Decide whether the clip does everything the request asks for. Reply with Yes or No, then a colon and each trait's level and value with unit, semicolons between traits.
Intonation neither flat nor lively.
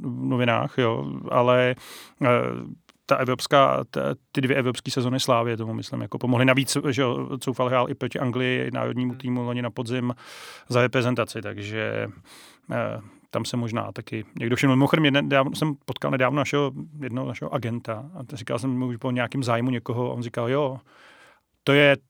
No: narrow, 2.3 semitones